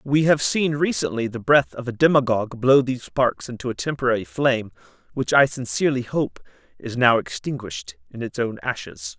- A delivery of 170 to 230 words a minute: Yes, average, 175 wpm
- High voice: No, low, 125 Hz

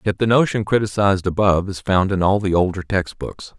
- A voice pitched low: Yes, low, 100 Hz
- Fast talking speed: Yes, fast, 220 wpm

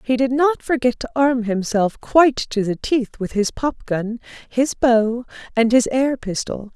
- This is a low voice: No, high, 240 Hz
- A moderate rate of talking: Yes, average, 185 wpm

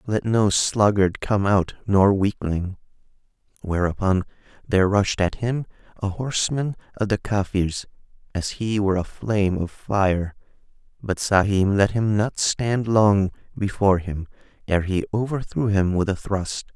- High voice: No, low, 100 Hz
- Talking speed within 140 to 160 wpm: Yes, average, 145 wpm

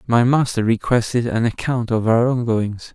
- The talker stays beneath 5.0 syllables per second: Yes, 4.7 syllables/s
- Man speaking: Yes, male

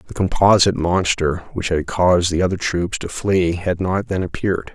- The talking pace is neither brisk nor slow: Yes, average, 190 wpm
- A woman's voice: No, male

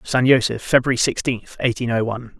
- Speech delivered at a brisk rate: No, average, 175 wpm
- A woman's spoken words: No, male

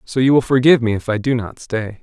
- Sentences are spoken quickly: Yes, fast, 295 wpm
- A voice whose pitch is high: No, low, 120 Hz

